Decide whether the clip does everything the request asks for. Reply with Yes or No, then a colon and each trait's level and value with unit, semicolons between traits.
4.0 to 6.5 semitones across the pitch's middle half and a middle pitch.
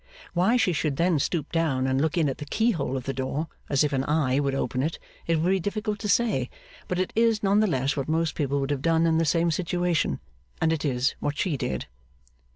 Yes: average, 4.5 semitones; medium, 160 Hz